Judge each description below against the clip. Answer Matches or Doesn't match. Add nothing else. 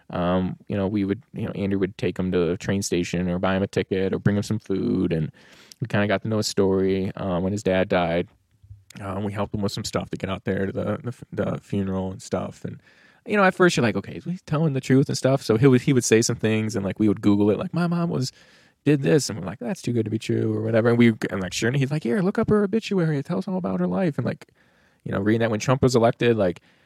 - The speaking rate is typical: Doesn't match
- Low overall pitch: Matches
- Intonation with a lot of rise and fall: Matches